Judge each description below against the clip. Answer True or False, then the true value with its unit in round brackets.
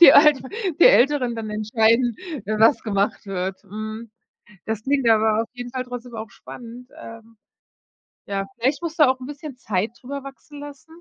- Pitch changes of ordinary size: True (3.9 semitones)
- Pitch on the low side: False (235 Hz)